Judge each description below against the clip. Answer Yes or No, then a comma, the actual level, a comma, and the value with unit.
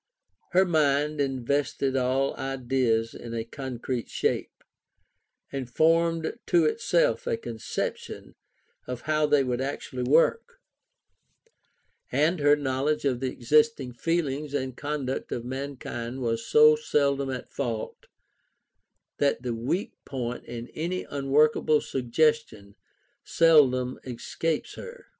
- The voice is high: No, medium, 140 Hz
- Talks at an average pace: No, slow, 115 wpm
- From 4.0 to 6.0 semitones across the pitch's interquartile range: No, average, 3.5 semitones